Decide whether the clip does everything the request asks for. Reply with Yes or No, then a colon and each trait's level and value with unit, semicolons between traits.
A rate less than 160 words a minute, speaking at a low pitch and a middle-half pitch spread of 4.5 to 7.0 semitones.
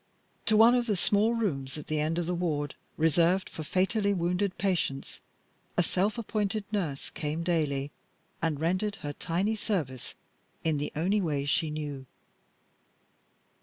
No: average, 150 wpm; medium, 170 Hz; average, 5.1 semitones